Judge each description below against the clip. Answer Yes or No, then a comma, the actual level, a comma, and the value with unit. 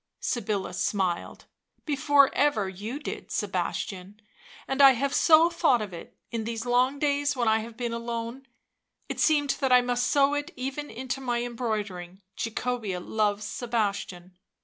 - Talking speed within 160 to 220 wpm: Yes, average, 165 wpm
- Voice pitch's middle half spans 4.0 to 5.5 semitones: Yes, average, 4.4 semitones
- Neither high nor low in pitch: No, high, 240 Hz